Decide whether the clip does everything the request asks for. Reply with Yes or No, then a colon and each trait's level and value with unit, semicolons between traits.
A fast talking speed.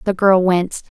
No: average, 180 wpm